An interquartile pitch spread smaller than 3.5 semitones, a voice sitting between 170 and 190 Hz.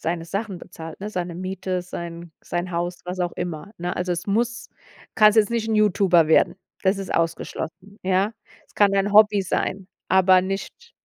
Yes: average, 2.8 semitones; medium, 185 Hz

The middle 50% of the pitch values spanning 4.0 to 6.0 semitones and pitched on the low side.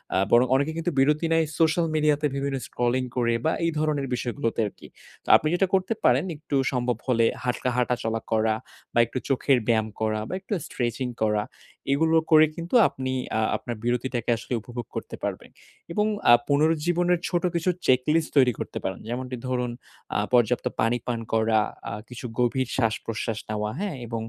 Yes: average, 4.7 semitones; low, 125 Hz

